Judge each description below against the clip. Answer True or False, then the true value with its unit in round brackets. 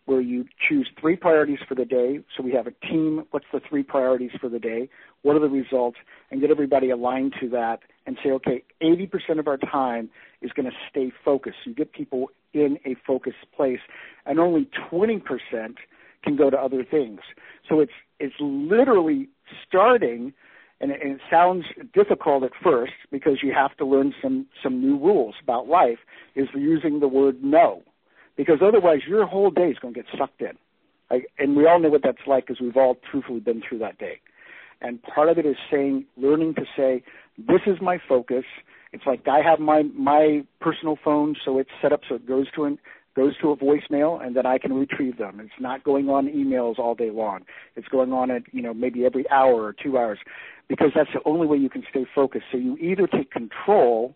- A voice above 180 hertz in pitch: False (140 Hz)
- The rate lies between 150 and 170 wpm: False (205 wpm)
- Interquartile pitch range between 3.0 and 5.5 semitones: True (3.3 semitones)